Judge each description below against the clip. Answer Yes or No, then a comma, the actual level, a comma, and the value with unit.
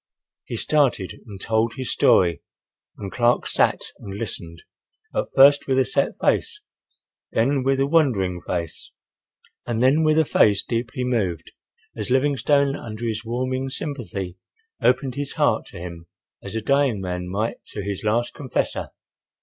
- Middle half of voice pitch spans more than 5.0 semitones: Yes, wide, 5.5 semitones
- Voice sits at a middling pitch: No, low, 120 Hz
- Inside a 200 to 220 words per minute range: No, average, 150 wpm